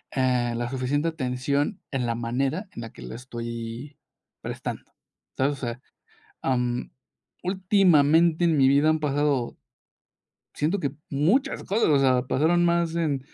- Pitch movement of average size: Yes, average, 4.5 semitones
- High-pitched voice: No, medium, 140 Hz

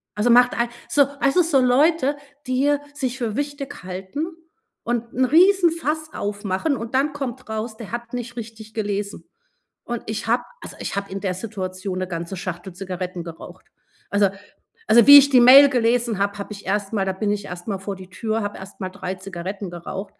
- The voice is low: No, high, 220 Hz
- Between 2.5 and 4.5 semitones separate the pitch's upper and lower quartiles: No, average, 4.9 semitones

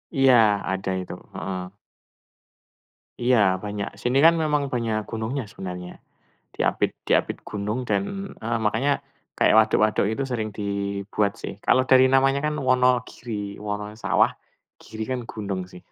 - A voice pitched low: Yes, low, 110 Hz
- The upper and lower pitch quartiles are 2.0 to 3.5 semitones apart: No, average, 4.2 semitones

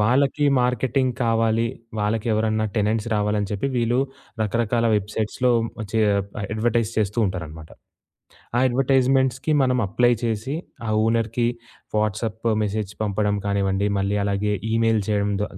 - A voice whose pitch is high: No, low, 110 Hz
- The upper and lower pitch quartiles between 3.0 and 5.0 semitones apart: No, narrow, 2.6 semitones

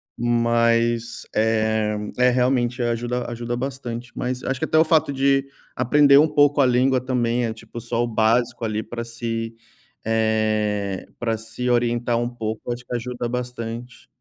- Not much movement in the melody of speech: Yes, narrow, 1.6 semitones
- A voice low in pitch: Yes, low, 120 Hz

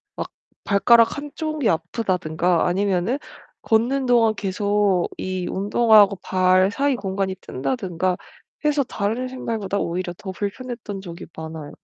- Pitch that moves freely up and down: No, average, 4.1 semitones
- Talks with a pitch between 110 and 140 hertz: No, high, 200 Hz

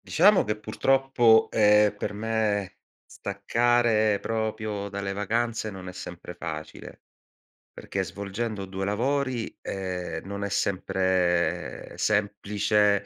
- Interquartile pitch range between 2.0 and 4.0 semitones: Yes, narrow, 2.4 semitones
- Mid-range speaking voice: No, low, 105 Hz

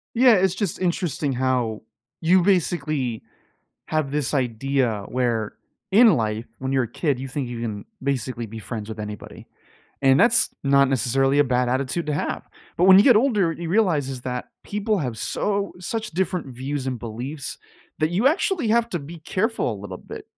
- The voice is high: No, medium, 140 Hz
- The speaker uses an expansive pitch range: Yes, wide, 6.8 semitones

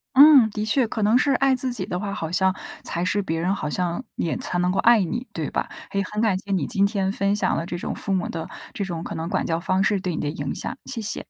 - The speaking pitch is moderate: No, high, 195 Hz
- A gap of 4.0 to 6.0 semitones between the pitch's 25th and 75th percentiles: No, average, 3.6 semitones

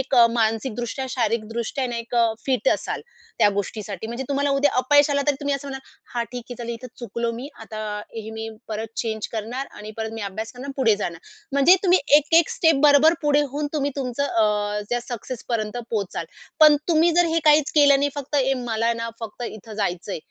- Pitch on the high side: Yes, high, 245 Hz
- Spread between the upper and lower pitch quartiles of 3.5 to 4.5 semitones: Yes, average, 4.2 semitones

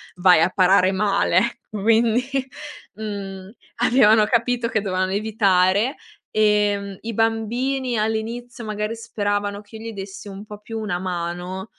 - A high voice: Yes, high, 210 Hz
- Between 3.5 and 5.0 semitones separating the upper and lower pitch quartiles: No, average, 2.7 semitones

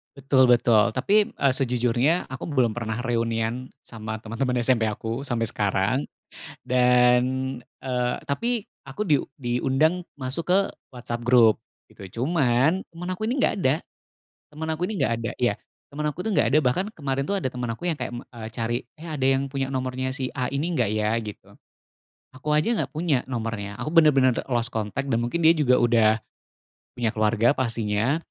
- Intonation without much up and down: No, average, 4.0 semitones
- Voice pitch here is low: Yes, low, 130 Hz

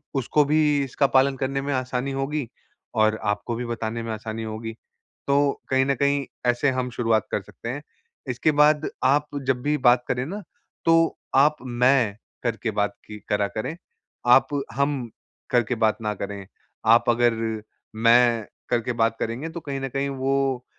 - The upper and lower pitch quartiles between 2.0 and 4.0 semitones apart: Yes, average, 3.4 semitones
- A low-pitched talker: Yes, low, 125 Hz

